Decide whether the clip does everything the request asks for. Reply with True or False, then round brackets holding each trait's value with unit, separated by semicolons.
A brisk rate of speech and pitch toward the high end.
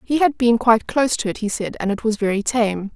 True (285 wpm; 225 Hz)